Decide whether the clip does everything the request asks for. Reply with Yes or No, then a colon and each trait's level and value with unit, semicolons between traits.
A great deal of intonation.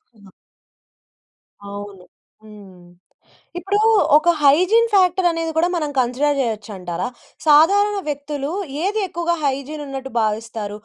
Yes: wide, 8.1 semitones